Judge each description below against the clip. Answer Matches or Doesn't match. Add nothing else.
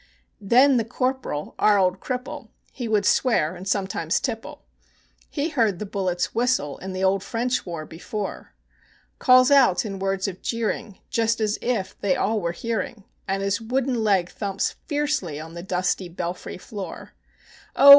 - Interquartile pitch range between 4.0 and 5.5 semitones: Matches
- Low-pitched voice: Doesn't match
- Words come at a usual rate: Matches